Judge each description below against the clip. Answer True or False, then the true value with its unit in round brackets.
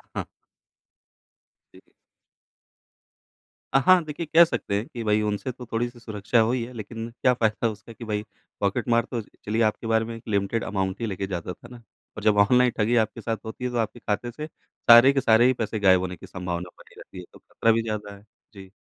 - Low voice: True (110 Hz)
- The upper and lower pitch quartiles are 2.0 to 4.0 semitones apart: True (2.8 semitones)